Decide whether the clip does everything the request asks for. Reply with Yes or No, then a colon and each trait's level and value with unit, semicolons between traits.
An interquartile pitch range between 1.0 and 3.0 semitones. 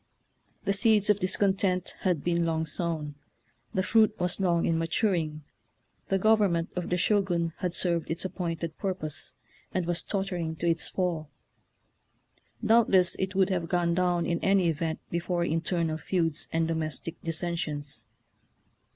Yes: narrow, 2.5 semitones